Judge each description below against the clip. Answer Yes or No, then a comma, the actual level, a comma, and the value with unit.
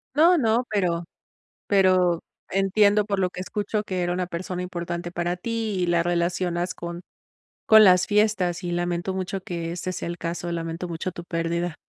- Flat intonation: Yes, narrow, 2.2 semitones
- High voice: No, medium, 180 Hz